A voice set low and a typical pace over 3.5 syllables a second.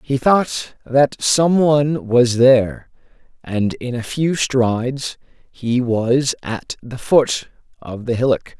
No: low, 125 Hz; 3.4 syllables/s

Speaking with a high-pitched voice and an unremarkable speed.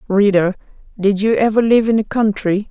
Yes: high, 210 Hz; average, 180 wpm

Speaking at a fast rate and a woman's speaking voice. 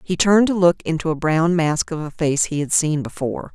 Yes: fast, 255 wpm; female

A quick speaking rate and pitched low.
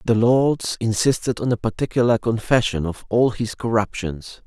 No: average, 150 wpm; low, 115 Hz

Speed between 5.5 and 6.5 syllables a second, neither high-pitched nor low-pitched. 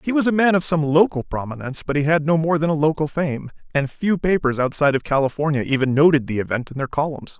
Yes: 6.4 syllables/s; medium, 150 Hz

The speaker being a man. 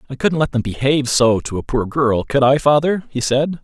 Yes: male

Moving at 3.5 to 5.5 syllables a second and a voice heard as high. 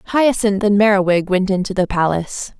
Yes: 5.1 syllables/s; high, 200 Hz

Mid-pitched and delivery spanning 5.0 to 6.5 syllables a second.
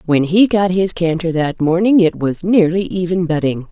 No: medium, 175 Hz; 4.8 syllables/s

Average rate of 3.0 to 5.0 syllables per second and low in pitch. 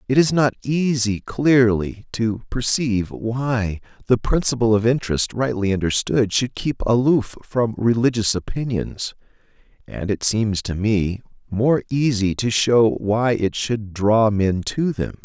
Yes: 4.0 syllables/s; low, 115 Hz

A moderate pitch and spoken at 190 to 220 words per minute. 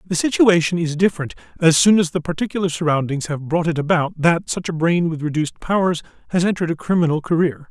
Yes: medium, 165 Hz; average, 200 wpm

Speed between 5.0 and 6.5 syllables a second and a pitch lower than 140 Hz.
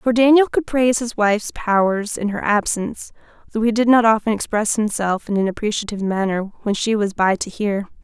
No: 5.5 syllables/s; high, 215 Hz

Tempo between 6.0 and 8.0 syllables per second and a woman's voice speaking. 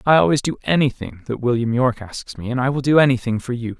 No: 6.5 syllables/s; male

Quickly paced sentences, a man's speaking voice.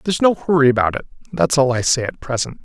Yes: fast, 250 wpm; male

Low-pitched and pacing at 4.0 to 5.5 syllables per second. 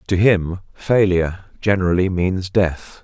Yes: very low, 95 Hz; 4.2 syllables/s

